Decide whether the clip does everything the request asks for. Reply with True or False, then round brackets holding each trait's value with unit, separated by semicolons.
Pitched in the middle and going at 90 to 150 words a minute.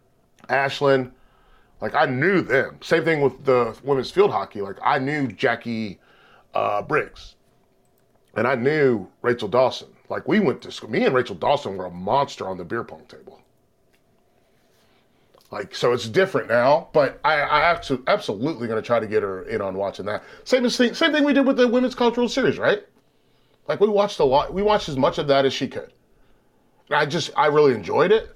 False (165 Hz; 190 wpm)